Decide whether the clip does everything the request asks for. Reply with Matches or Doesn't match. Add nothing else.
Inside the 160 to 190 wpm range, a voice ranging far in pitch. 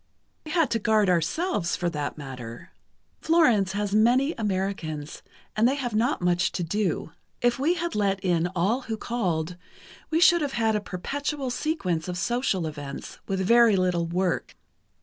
Matches